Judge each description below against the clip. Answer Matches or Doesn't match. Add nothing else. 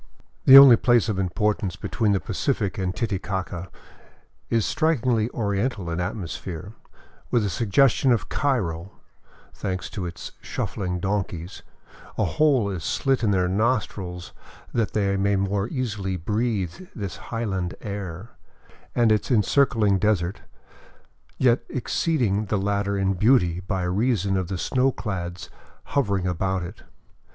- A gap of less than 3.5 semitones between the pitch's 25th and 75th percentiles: Doesn't match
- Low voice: Matches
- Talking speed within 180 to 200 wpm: Doesn't match